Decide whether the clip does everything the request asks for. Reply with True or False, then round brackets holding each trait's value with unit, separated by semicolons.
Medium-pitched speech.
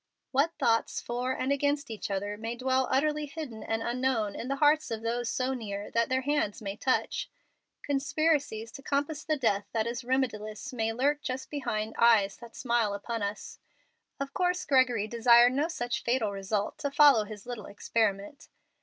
False (240 Hz)